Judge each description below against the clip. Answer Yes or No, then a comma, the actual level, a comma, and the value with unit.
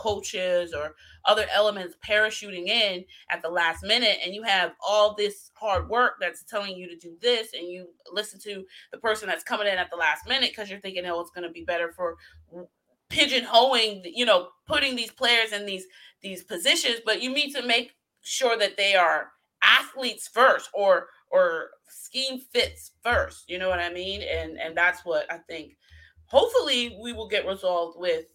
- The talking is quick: No, average, 190 wpm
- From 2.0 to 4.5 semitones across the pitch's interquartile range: No, average, 5.2 semitones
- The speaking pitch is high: Yes, high, 205 Hz